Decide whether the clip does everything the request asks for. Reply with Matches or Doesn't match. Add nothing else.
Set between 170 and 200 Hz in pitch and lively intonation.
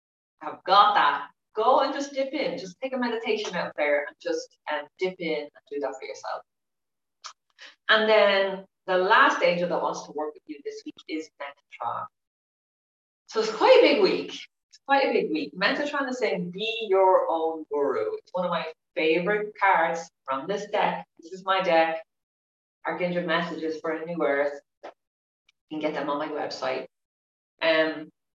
Matches